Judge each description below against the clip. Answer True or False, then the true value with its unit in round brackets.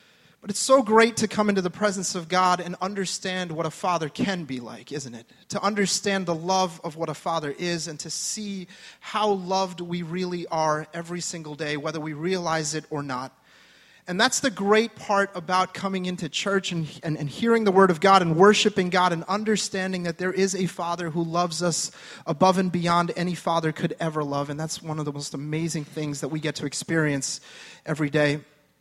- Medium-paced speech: False (210 wpm)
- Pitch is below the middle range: False (175 Hz)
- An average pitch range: True (3.3 semitones)